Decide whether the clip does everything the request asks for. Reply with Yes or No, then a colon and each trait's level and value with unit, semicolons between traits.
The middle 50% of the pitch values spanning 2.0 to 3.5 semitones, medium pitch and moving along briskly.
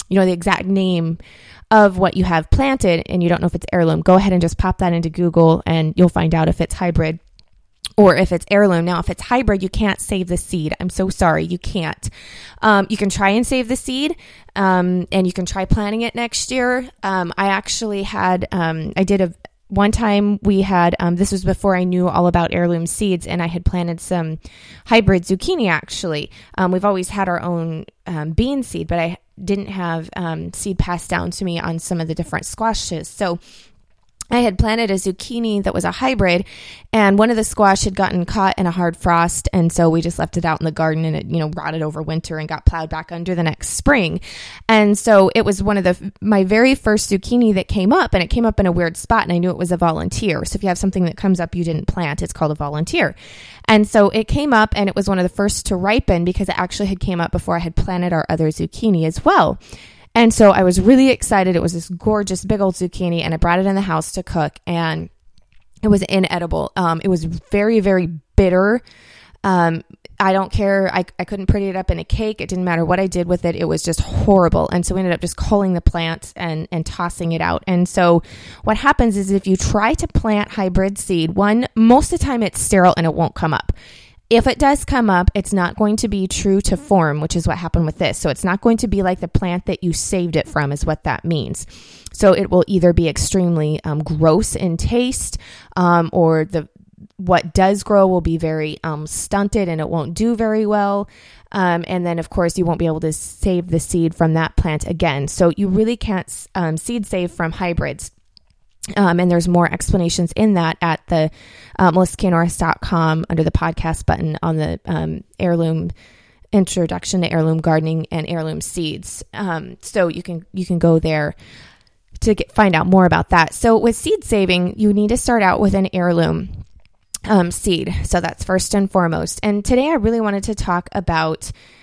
Yes: average, 3.2 semitones; medium, 180 Hz; fast, 225 wpm